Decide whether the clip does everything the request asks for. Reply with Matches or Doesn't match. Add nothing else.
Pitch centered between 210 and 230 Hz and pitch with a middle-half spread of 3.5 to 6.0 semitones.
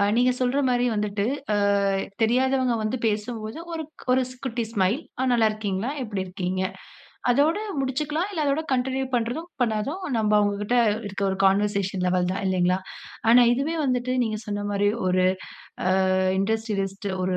Matches